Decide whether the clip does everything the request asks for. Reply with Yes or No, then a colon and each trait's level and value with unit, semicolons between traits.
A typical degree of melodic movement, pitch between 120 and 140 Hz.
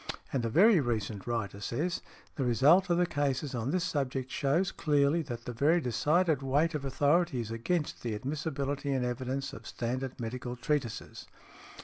Yes: average, 4.1 semitones; low, 135 Hz